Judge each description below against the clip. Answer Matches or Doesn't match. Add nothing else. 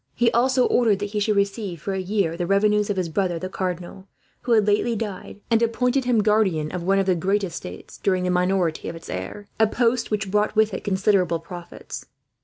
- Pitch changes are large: Doesn't match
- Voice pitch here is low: Doesn't match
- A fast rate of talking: Matches